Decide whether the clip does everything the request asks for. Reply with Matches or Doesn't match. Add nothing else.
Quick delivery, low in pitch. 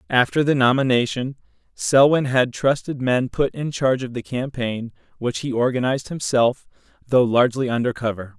Doesn't match